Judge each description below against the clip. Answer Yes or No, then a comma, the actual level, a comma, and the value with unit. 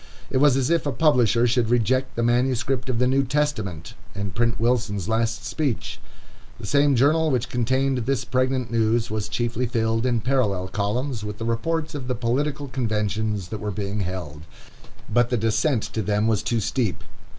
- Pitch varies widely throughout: No, average, 3.2 semitones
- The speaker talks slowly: No, average, 180 wpm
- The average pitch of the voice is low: Yes, low, 120 Hz